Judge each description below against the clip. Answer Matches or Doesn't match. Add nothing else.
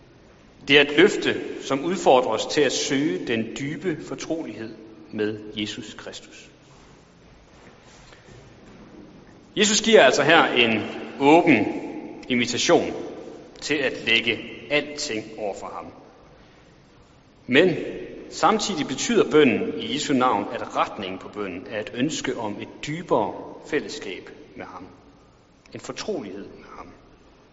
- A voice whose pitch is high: Doesn't match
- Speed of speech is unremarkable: Doesn't match